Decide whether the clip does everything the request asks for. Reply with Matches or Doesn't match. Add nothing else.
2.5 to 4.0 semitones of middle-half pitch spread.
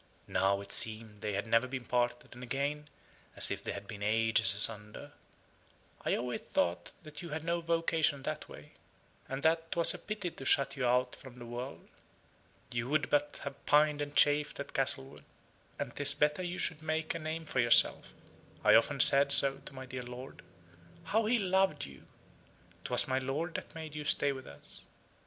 Doesn't match